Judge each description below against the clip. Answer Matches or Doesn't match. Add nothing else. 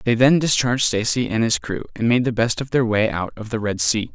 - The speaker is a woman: Doesn't match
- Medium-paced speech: Doesn't match